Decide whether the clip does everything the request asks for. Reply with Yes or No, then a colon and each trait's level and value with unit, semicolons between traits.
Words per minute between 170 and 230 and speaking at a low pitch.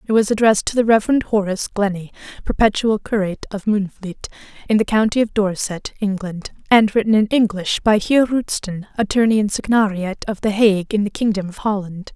No: average, 180 wpm; high, 205 Hz